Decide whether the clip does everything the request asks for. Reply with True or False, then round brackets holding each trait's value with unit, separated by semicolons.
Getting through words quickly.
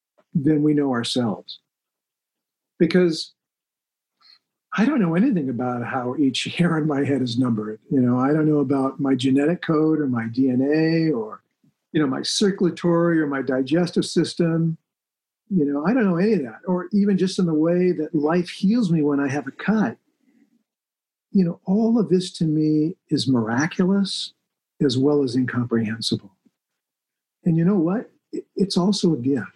False (170 wpm)